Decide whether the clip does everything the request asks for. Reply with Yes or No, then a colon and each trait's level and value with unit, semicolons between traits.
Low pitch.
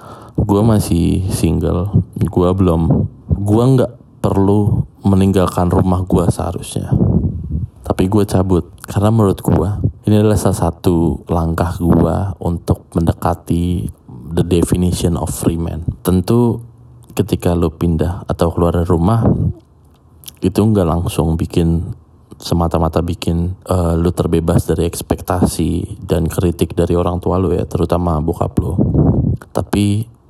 Yes: very low, 90 Hz